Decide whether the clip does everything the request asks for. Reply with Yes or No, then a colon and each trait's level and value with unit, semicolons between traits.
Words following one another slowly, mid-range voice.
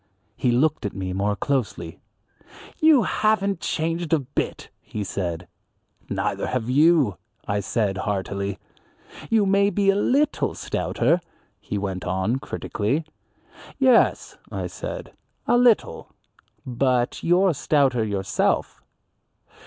No: slow, 115 wpm; low, 130 Hz